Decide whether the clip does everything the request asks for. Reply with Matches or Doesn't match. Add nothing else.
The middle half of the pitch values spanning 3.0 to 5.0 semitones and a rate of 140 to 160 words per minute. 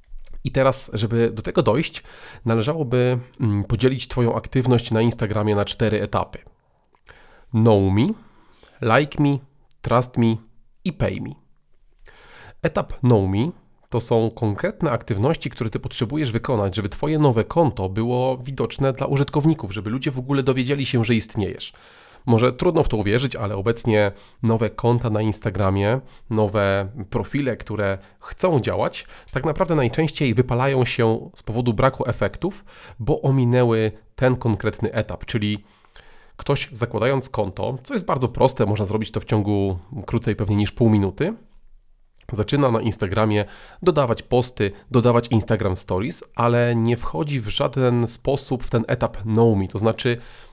Matches